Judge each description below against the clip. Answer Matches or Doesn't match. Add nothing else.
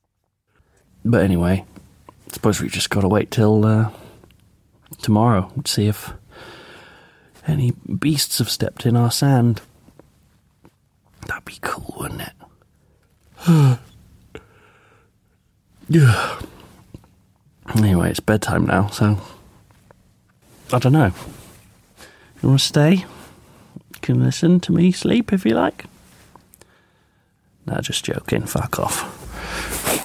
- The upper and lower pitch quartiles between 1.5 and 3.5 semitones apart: Doesn't match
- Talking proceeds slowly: Matches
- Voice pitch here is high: Doesn't match